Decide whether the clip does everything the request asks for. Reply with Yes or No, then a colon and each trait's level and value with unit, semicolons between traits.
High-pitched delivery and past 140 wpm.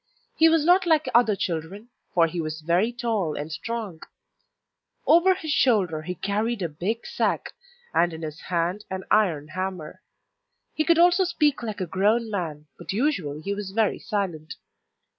Yes: high, 200 Hz; average, 165 wpm